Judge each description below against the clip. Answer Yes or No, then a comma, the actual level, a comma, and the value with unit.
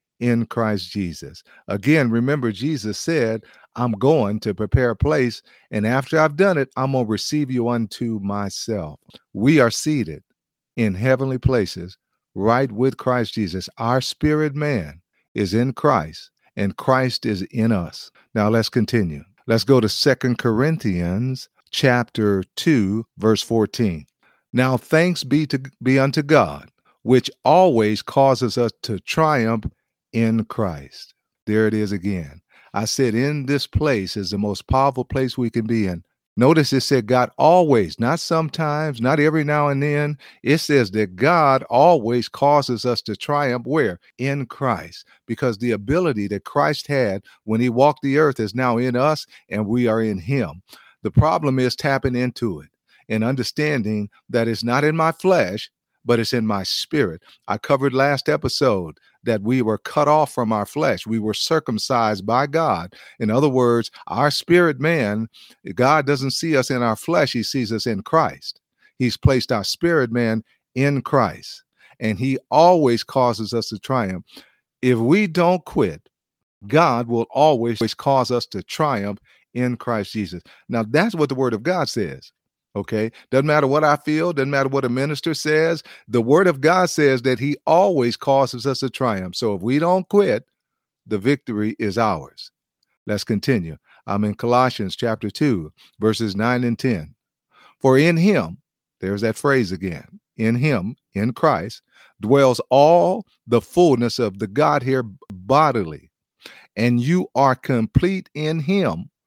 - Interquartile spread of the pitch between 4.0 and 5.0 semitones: Yes, average, 4.5 semitones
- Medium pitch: No, low, 125 Hz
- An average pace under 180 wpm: Yes, average, 160 wpm